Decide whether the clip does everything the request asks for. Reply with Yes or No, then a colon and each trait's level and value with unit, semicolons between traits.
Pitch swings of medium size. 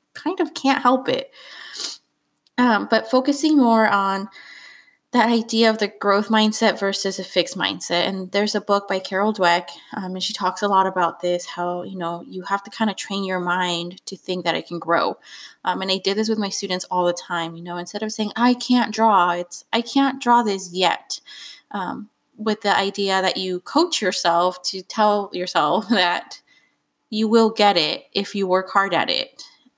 Yes: average, 4.1 semitones